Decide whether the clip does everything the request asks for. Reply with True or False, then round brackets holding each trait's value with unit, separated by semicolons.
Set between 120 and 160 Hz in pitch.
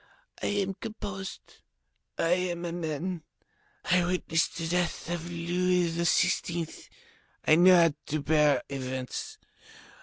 False (170 Hz)